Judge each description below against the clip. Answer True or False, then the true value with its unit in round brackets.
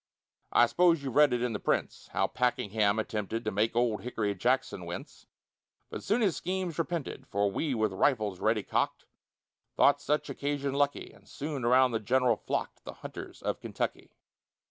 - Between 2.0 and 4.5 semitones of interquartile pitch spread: False (4.9 semitones)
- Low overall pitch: True (125 Hz)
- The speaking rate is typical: True (170 wpm)